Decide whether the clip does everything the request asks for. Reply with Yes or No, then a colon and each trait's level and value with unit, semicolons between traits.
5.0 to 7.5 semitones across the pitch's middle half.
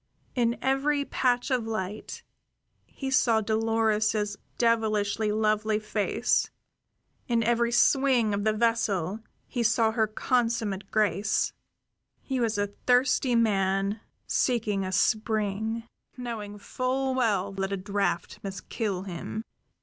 No: average, 2.7 semitones